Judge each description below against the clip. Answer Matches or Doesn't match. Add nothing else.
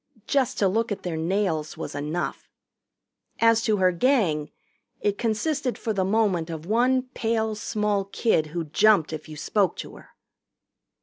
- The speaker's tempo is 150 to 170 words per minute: Matches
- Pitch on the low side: Doesn't match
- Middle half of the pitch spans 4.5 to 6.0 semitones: Matches